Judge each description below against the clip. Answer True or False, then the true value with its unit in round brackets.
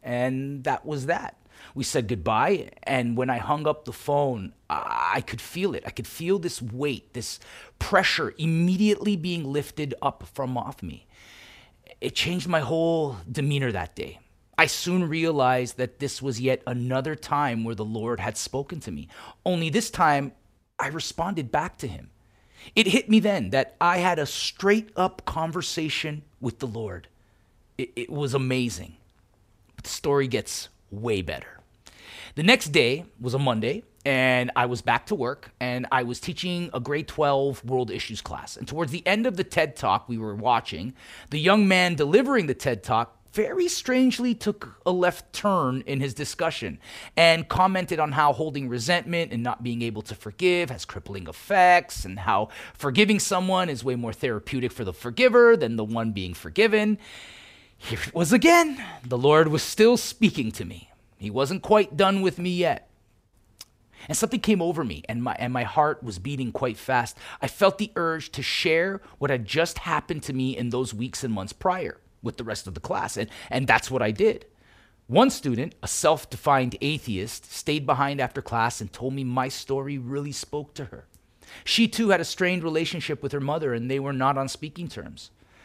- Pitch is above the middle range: False (140 Hz)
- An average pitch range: False (6.4 semitones)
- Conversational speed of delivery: True (185 wpm)